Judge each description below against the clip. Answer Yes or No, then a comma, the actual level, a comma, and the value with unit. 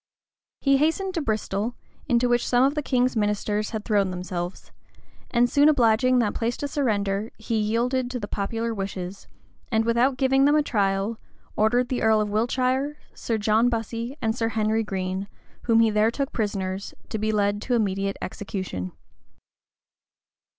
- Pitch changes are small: No, average, 3.3 semitones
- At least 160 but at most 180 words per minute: Yes, average, 165 wpm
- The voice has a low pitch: No, high, 225 Hz